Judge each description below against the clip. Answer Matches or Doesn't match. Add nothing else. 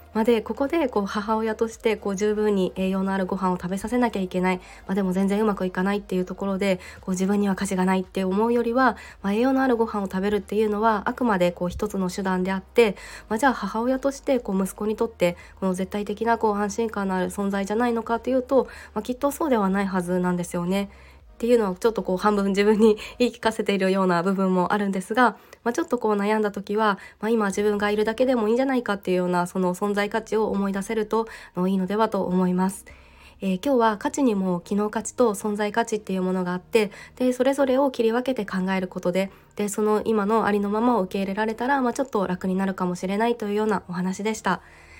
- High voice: Matches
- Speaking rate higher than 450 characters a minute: Matches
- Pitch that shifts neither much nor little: Matches